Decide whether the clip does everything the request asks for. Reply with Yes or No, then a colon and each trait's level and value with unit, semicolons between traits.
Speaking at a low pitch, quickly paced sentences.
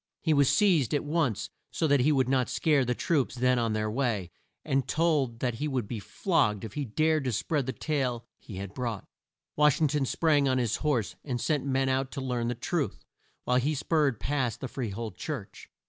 Yes: low, 130 Hz; fast, 215 wpm